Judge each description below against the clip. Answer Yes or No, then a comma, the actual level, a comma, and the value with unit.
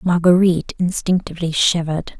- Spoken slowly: Yes, slow, 80 wpm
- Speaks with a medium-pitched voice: Yes, medium, 175 Hz